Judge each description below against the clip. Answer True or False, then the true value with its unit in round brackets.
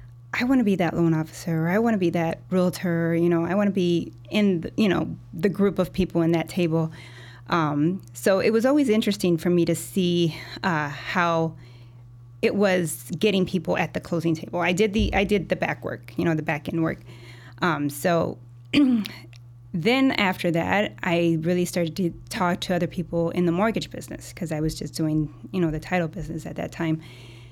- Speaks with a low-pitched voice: False (170 Hz)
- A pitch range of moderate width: True (3.3 semitones)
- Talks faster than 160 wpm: True (205 wpm)